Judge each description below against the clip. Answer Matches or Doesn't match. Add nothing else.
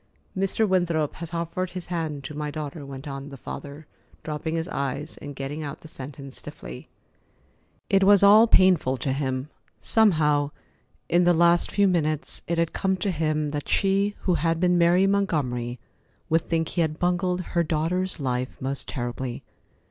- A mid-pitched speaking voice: Matches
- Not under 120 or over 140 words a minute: Doesn't match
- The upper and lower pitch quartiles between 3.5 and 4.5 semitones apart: Matches